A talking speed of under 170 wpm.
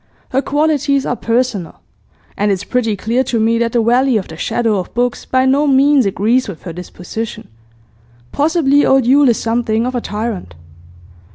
No: average, 175 wpm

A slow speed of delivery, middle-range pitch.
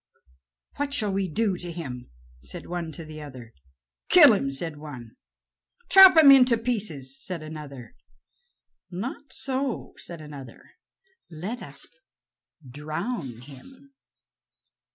Yes: slow, 115 wpm; medium, 170 Hz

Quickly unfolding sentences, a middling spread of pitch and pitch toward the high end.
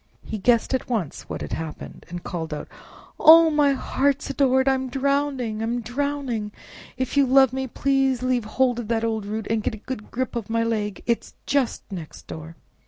No: average, 185 wpm; average, 3.8 semitones; high, 245 Hz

